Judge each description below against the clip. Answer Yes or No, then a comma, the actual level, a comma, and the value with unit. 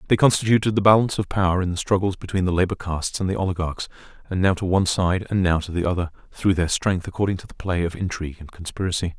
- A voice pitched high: No, very low, 90 Hz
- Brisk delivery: Yes, fast, 240 wpm